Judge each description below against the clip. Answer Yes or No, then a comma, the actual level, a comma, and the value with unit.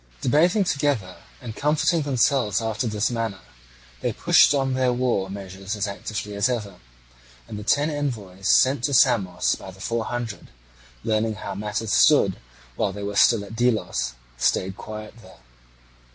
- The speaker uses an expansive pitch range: No, average, 4.2 semitones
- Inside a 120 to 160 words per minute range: Yes, average, 155 wpm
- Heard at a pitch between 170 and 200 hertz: No, low, 110 Hz